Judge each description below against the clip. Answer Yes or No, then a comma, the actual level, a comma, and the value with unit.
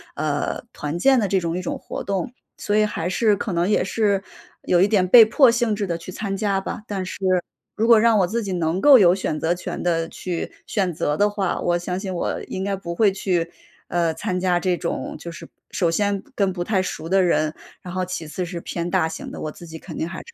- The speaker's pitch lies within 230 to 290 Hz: No, medium, 185 Hz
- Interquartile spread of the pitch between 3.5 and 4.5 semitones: No, average, 3.0 semitones